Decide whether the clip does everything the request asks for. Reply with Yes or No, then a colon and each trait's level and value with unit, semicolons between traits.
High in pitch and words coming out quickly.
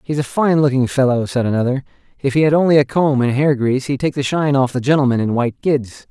No: low, 135 Hz; fast, 255 wpm